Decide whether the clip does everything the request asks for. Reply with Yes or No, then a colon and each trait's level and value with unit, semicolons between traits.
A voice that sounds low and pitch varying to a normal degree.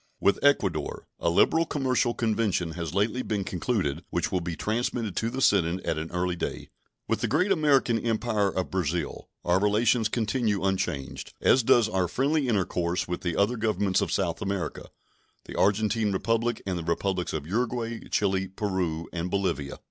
Yes: low, 100 Hz; average, 4.6 semitones